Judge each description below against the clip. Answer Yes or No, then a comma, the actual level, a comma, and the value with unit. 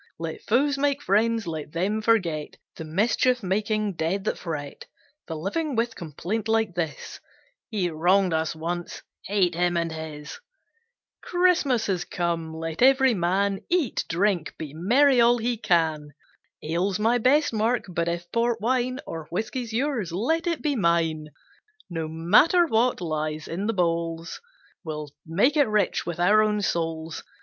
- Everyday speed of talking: Yes, average, 155 wpm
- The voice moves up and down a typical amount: No, wide, 6.1 semitones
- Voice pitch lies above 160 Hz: Yes, high, 190 Hz